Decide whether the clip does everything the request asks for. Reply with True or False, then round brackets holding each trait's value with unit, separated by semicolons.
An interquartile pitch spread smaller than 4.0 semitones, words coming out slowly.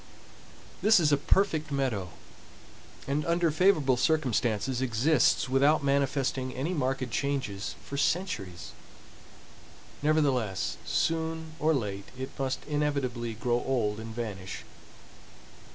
False (4.4 semitones; 105 wpm)